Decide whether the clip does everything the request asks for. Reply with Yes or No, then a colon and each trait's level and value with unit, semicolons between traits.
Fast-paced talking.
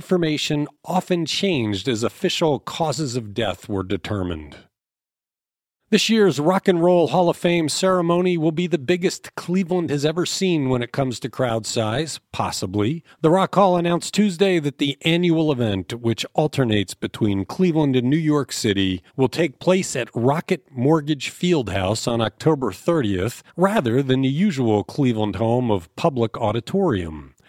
No: average, 155 wpm